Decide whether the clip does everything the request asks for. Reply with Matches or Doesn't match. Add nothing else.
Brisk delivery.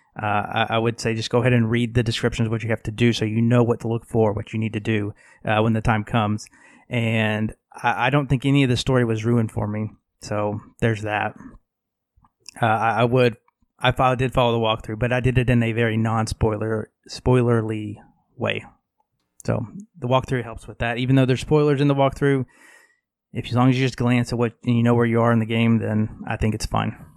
Matches